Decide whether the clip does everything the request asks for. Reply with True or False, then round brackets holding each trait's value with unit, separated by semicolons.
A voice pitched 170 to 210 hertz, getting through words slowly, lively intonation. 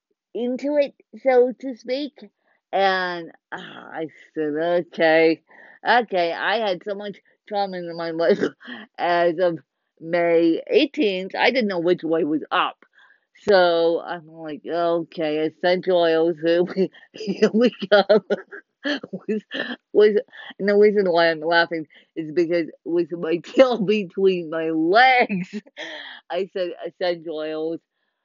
True (185 Hz; 125 wpm; 6.4 semitones)